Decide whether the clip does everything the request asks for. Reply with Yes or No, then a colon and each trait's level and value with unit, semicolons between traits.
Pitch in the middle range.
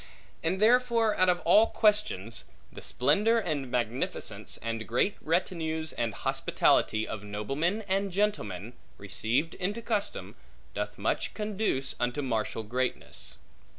Yes: medium, 160 Hz